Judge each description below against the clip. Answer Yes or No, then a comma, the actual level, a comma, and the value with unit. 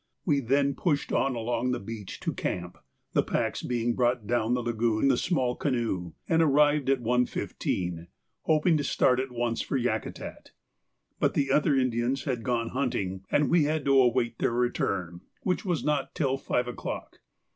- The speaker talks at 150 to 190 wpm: Yes, average, 175 wpm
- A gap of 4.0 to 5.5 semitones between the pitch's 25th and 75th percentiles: No, average, 3.3 semitones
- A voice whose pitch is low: Yes, low, 125 Hz